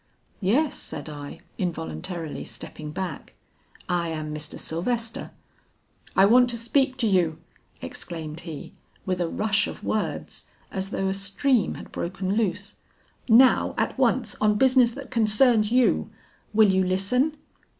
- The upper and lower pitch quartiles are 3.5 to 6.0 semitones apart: Yes, average, 5.2 semitones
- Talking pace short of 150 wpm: Yes, average, 140 wpm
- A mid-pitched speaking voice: No, high, 195 Hz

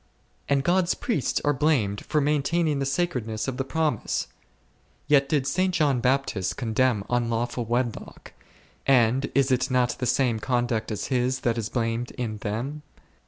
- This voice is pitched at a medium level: No, low, 130 Hz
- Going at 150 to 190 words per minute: Yes, average, 160 wpm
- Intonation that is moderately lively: Yes, average, 3.3 semitones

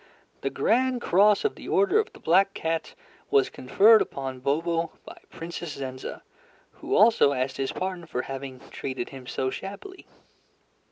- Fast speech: No, average, 155 wpm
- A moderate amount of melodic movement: No, wide, 8.0 semitones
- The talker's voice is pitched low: No, medium, 165 Hz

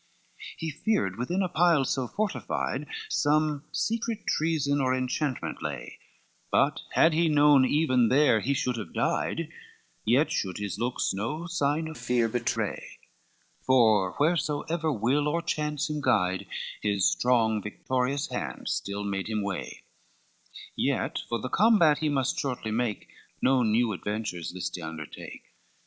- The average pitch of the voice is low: Yes, low, 130 Hz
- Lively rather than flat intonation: Yes, wide, 5.8 semitones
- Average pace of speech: Yes, average, 145 wpm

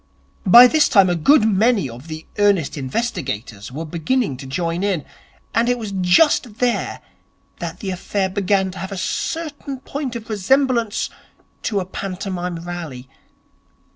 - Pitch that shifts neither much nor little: No, wide, 5.7 semitones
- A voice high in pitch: Yes, high, 195 Hz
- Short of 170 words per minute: Yes, average, 145 wpm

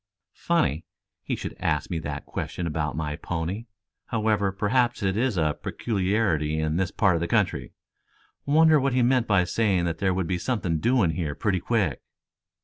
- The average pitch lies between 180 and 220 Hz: No, very low, 95 Hz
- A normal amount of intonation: No, wide, 5.7 semitones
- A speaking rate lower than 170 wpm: No, average, 175 wpm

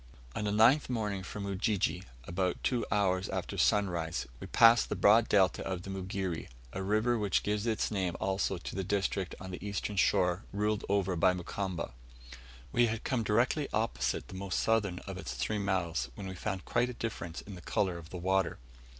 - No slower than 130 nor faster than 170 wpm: No, average, 195 wpm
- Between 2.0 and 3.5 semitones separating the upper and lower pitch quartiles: Yes, narrow, 2.6 semitones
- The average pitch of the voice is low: Yes, low, 100 Hz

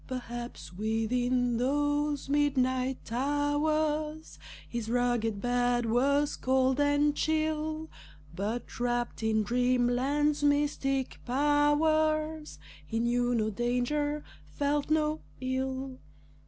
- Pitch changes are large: No, average, 3.3 semitones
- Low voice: No, very high, 265 Hz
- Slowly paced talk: Yes, slow, 90 wpm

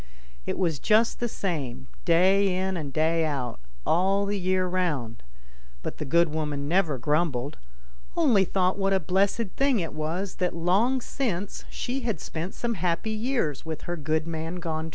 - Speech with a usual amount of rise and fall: Yes, average, 3.9 semitones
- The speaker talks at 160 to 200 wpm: Yes, average, 170 wpm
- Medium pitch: Yes, medium, 175 Hz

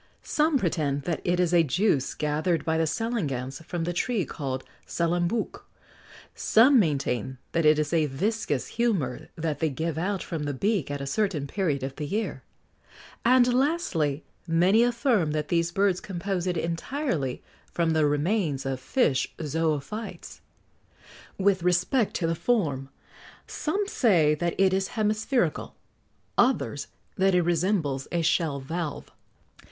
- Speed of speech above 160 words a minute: No, average, 145 wpm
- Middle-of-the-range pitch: Yes, medium, 170 Hz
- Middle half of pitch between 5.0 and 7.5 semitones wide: Yes, wide, 5.5 semitones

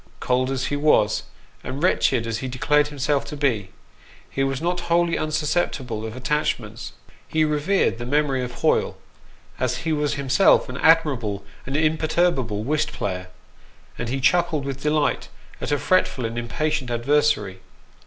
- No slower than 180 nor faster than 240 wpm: No, average, 155 wpm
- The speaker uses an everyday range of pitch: Yes, average, 4.1 semitones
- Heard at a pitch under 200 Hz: Yes, medium, 140 Hz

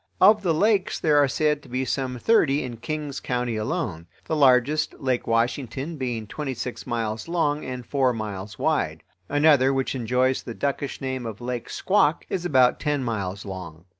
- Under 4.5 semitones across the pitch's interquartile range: Yes, average, 4.0 semitones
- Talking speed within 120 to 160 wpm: No, average, 175 wpm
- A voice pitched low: Yes, low, 130 Hz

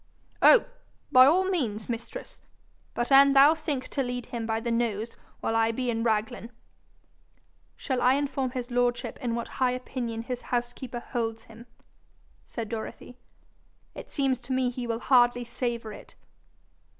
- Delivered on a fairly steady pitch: Yes, narrow, 2.1 semitones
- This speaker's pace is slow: No, average, 160 wpm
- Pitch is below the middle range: No, high, 245 Hz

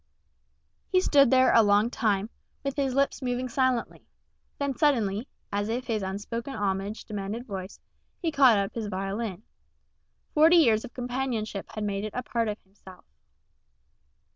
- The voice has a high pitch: Yes, high, 230 Hz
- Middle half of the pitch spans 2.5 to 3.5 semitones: No, average, 4.2 semitones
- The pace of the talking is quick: No, average, 150 wpm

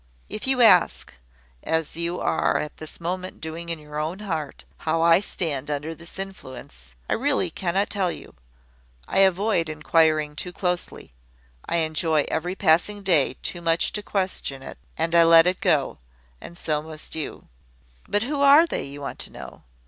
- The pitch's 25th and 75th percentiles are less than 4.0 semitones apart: Yes, average, 3.4 semitones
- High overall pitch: No, medium, 165 Hz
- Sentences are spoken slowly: No, average, 170 wpm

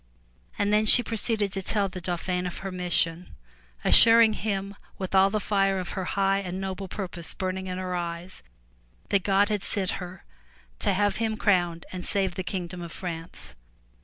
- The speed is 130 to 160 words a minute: No, average, 185 wpm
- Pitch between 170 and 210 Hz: Yes, high, 190 Hz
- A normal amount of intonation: No, narrow, 2.0 semitones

